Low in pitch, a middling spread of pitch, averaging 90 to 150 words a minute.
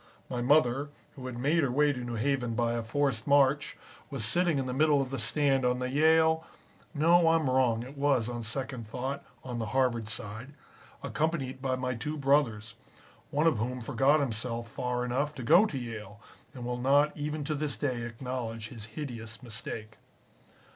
No: low, 130 Hz; average, 3.6 semitones; average, 185 wpm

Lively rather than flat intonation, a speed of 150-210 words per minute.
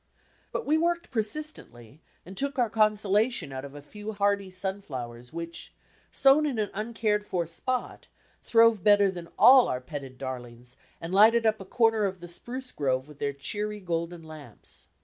Yes: wide, 7.1 semitones; average, 170 wpm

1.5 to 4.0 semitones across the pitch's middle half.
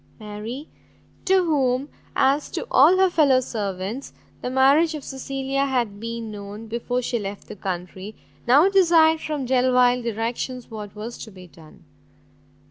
No: average, 4.6 semitones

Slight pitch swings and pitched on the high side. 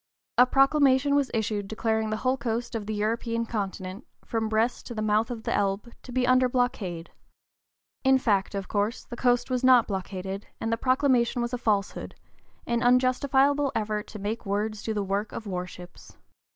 No: average, 3.4 semitones; high, 225 Hz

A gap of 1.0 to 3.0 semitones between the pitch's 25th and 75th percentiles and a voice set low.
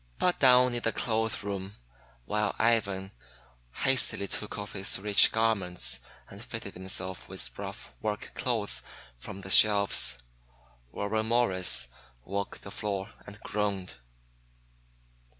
Yes: narrow, 2.6 semitones; low, 100 Hz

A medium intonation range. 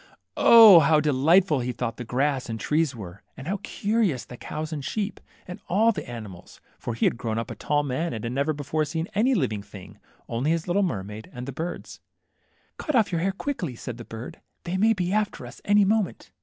No: wide, 7.7 semitones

